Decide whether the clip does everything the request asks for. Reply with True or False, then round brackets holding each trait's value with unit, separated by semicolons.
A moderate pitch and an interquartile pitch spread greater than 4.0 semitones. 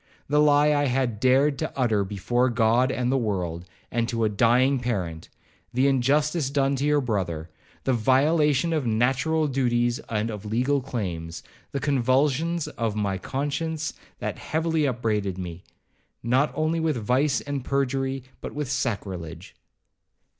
False (130 Hz; 4.7 semitones)